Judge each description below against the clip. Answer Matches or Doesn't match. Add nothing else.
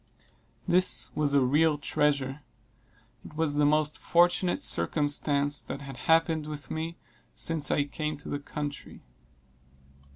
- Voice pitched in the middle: Matches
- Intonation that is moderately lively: Doesn't match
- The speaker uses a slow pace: Matches